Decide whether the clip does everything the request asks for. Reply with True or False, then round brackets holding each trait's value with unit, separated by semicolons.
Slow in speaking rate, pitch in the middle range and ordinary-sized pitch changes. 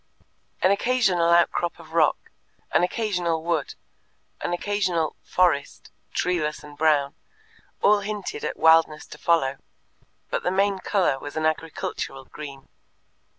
True (125 wpm; 170 Hz; 3.6 semitones)